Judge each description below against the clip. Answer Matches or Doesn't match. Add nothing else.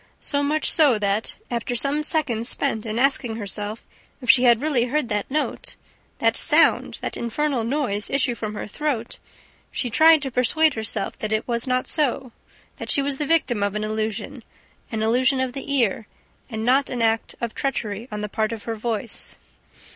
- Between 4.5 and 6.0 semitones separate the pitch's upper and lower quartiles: Doesn't match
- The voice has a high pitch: Matches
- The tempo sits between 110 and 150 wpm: Doesn't match